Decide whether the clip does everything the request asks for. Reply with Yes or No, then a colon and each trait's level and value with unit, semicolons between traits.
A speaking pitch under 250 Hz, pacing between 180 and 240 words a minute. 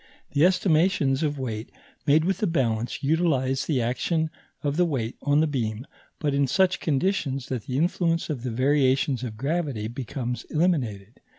No: medium, 140 Hz; average, 165 wpm